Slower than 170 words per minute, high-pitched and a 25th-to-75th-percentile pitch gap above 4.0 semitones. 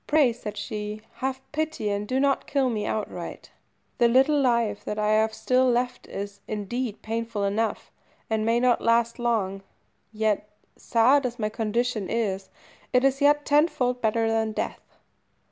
No: average, 160 wpm; high, 230 Hz; average, 3.1 semitones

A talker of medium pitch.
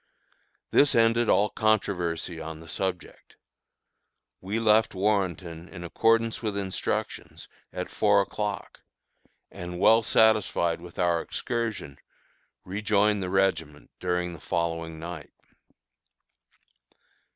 No: very low, 95 Hz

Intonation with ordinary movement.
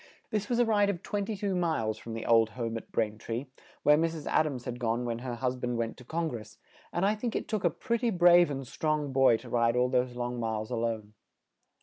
No: wide, 6.9 semitones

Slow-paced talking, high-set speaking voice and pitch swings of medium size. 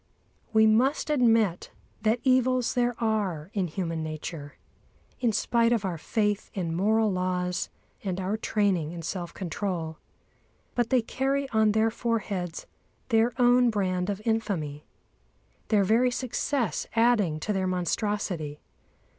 Yes: slow, 130 wpm; high, 210 Hz; average, 4.3 semitones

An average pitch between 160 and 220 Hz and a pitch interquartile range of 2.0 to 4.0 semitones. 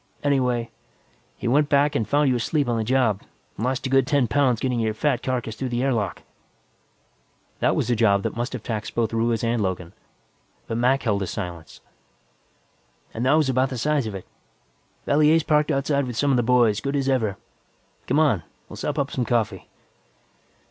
No: low, 125 Hz; average, 3.7 semitones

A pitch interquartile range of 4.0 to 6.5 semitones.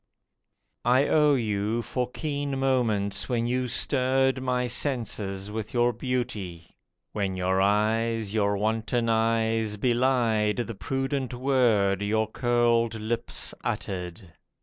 No: average, 3.2 semitones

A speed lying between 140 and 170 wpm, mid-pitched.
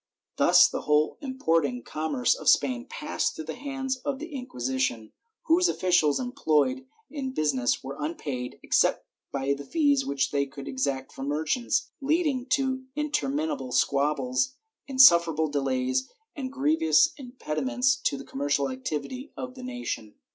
Yes: average, 145 wpm; medium, 160 Hz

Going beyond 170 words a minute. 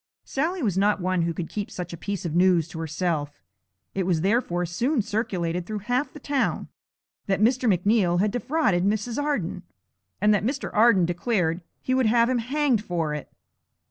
Yes: average, 180 wpm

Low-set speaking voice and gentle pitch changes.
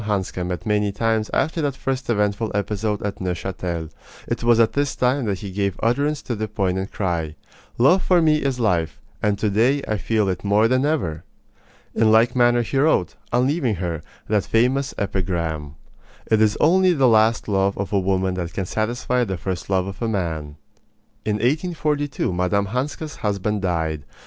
No: low, 105 Hz; average, 4.8 semitones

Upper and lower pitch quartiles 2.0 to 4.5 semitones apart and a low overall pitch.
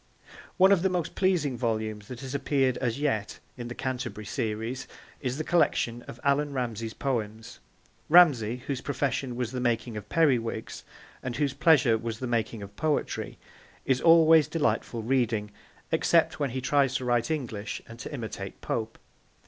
Yes: average, 4.0 semitones; low, 125 Hz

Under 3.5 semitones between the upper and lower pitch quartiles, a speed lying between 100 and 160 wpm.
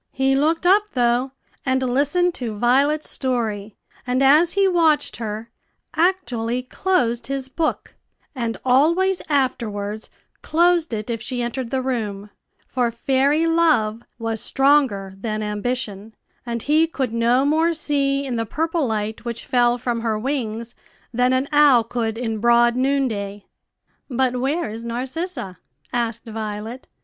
No: average, 4.1 semitones; average, 140 wpm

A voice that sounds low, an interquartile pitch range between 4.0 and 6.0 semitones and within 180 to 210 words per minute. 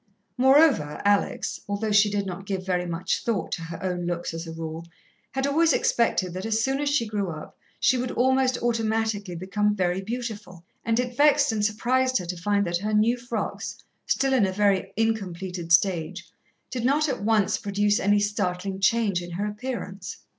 No: high, 205 Hz; average, 4.6 semitones; average, 185 wpm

